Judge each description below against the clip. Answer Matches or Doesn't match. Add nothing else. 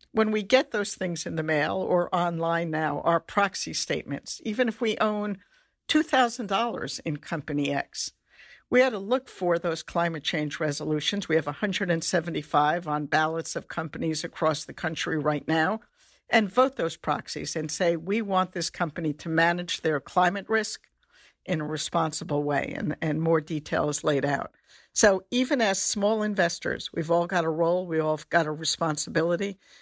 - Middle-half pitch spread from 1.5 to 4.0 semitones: Doesn't match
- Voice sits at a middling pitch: Matches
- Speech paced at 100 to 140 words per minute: Doesn't match